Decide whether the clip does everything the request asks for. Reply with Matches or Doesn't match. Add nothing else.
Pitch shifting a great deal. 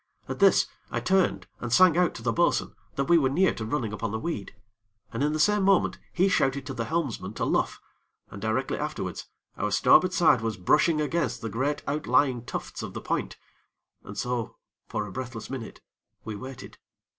Matches